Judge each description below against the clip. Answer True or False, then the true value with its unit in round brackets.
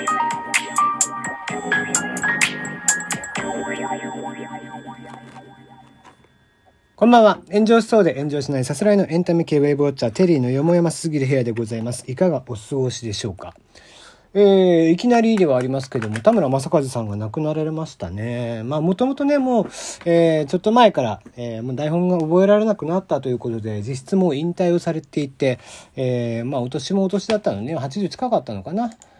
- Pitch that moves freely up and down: True (7.9 semitones)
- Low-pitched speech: False (160 Hz)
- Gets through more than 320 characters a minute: True (345 characters per minute)